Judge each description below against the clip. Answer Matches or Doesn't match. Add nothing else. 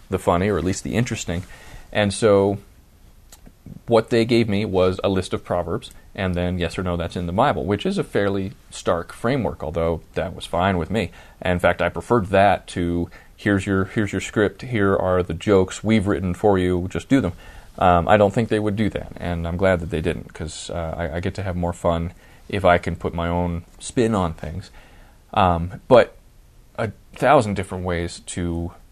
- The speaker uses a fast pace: Matches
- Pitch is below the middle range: Matches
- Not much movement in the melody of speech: Doesn't match